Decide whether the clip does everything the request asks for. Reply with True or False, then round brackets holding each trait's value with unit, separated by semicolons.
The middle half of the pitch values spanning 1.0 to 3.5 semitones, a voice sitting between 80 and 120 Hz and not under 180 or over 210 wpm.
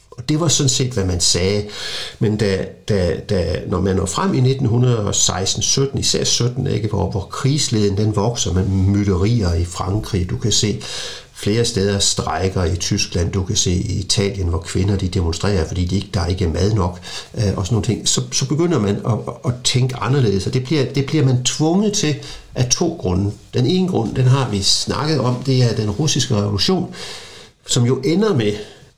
False (4.9 semitones; 105 Hz; 195 wpm)